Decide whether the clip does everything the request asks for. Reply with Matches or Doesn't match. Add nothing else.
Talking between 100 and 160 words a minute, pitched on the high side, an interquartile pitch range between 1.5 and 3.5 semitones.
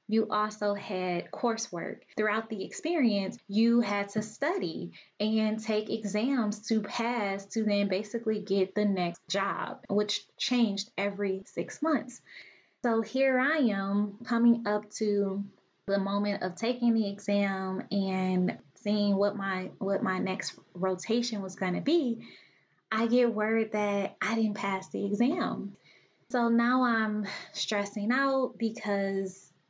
Matches